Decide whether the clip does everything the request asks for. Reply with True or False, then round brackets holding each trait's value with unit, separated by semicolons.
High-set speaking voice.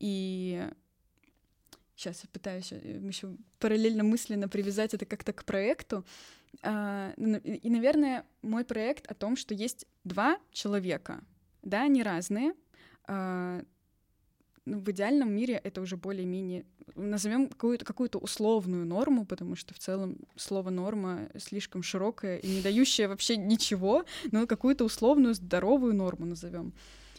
True (210 Hz)